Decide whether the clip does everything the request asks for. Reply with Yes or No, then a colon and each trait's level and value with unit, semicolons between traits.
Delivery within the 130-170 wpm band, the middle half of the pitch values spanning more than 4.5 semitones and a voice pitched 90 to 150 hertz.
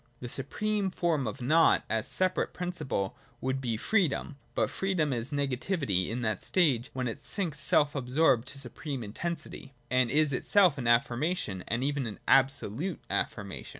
Yes: average, 160 wpm; average, 5.1 semitones; low, 135 Hz